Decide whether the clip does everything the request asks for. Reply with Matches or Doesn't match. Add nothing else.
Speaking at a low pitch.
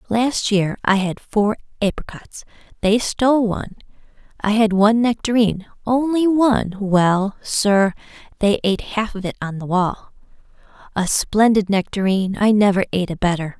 Doesn't match